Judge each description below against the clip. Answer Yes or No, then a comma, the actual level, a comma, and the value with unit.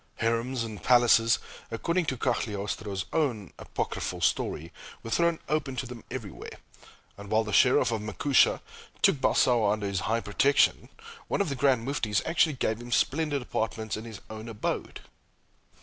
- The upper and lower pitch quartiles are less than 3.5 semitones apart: No, average, 4.0 semitones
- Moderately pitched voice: No, low, 115 Hz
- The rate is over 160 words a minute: No, average, 155 wpm